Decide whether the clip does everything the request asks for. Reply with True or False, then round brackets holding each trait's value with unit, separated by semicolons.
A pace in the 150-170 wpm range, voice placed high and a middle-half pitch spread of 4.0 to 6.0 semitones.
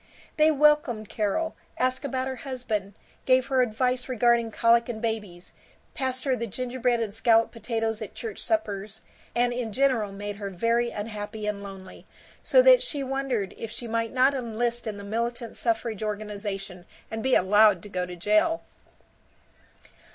False (160 wpm; 230 Hz; 3.5 semitones)